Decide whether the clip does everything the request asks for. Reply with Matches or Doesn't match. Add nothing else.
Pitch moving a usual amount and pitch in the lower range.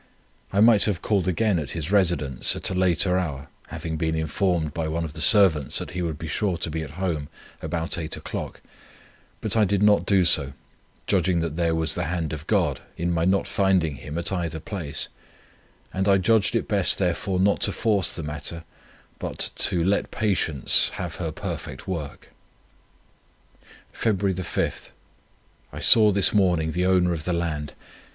Matches